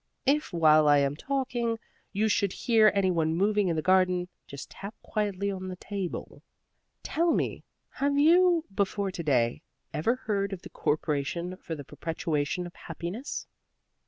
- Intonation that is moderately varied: Yes, average, 5.0 semitones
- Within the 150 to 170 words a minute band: Yes, average, 160 wpm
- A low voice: No, medium, 185 Hz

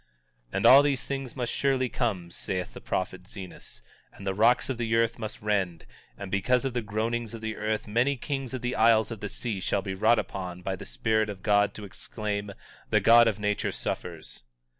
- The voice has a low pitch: Yes, low, 110 Hz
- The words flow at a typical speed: No, fast, 220 wpm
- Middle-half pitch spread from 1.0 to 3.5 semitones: Yes, average, 3.1 semitones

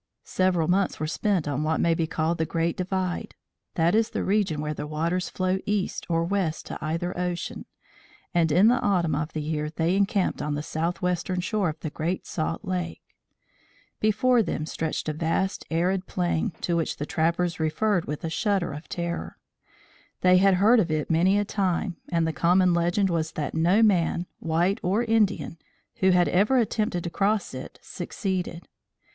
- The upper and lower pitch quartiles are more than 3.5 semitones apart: No, average, 3.0 semitones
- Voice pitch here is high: No, medium, 175 Hz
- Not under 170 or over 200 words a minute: Yes, average, 180 wpm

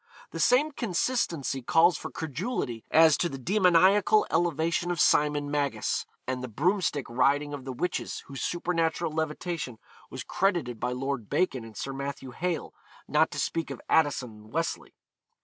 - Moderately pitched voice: Yes, medium, 155 Hz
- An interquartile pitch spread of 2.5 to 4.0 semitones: No, average, 4.4 semitones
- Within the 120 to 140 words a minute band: No, average, 155 wpm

